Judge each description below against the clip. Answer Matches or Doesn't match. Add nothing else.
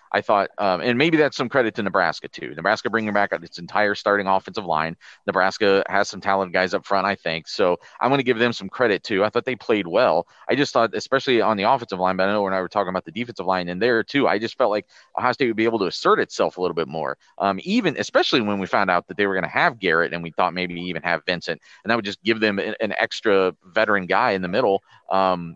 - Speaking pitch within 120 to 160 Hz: Doesn't match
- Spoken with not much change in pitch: Doesn't match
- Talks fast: Matches